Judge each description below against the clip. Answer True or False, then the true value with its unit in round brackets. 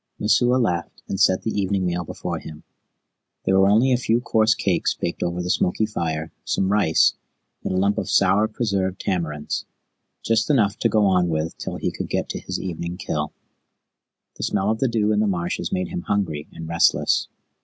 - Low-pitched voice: True (95 Hz)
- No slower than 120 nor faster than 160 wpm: False (195 wpm)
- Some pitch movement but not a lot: True (3.7 semitones)